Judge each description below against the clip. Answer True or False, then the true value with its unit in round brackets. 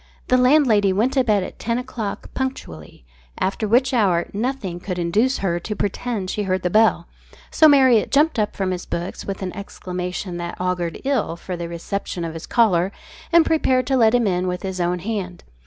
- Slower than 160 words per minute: False (195 wpm)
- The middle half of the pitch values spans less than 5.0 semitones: False (5.5 semitones)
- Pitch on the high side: True (200 Hz)